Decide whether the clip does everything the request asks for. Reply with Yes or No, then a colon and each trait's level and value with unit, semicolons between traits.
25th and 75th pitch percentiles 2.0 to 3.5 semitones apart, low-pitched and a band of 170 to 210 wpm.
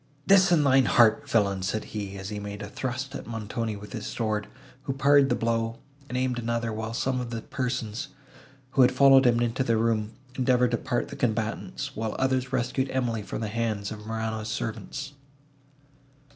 Yes: average, 3.1 semitones; low, 115 Hz; average, 185 wpm